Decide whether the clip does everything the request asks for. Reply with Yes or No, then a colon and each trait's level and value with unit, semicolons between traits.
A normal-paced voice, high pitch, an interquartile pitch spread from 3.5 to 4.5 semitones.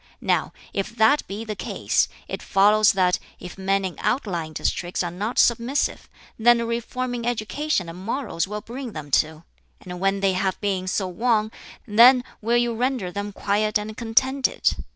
Yes: average, 170 wpm; high, 210 Hz; average, 3.9 semitones